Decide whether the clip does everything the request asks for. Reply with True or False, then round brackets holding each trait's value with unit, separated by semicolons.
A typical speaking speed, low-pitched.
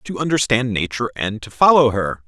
True (185 wpm; 115 Hz)